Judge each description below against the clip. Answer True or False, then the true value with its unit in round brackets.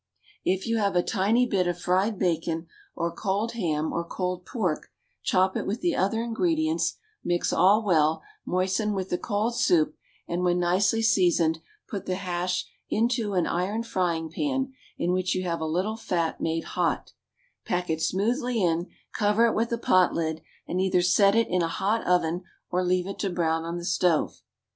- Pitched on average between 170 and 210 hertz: True (185 Hz)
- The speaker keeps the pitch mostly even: False (3.6 semitones)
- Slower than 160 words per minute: False (185 wpm)